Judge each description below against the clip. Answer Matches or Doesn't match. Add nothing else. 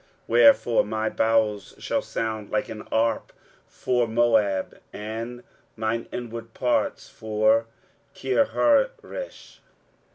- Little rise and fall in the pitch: Matches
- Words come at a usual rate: Doesn't match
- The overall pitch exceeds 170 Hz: Doesn't match